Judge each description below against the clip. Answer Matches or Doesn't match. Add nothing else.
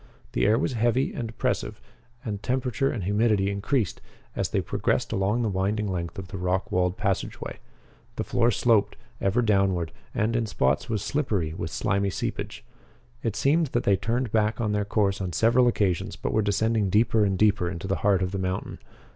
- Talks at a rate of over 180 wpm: Matches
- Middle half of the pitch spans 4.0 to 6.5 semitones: Doesn't match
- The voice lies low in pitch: Matches